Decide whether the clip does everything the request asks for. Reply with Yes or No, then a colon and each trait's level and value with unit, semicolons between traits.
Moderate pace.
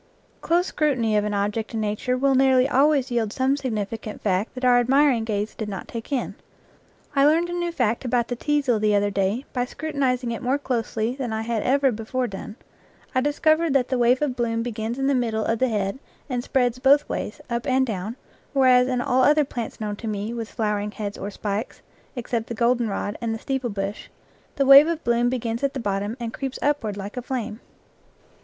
No: fast, 210 wpm